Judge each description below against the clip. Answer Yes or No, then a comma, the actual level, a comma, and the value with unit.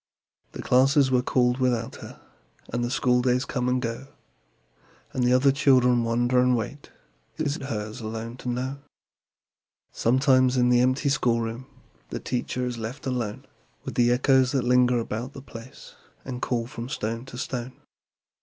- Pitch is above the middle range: No, low, 125 Hz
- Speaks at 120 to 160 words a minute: Yes, average, 155 wpm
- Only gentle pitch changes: Yes, narrow, 1.6 semitones